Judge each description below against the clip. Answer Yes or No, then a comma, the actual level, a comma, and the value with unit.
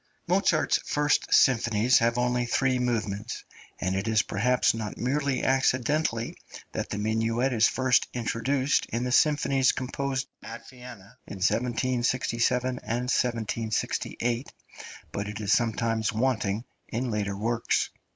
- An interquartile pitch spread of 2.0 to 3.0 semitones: Yes, narrow, 2.6 semitones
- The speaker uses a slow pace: Yes, slow, 125 wpm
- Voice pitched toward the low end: Yes, low, 120 Hz